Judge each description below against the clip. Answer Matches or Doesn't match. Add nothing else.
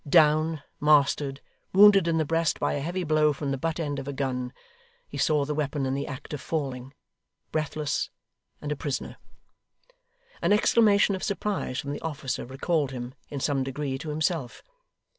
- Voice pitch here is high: Doesn't match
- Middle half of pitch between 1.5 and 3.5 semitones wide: Matches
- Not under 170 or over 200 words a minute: Matches